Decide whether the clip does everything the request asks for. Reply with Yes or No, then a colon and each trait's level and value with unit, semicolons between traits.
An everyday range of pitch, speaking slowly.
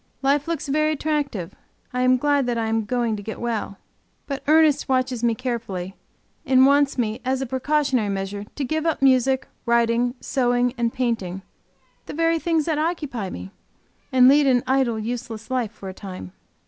No: average, 4.0 semitones; average, 175 wpm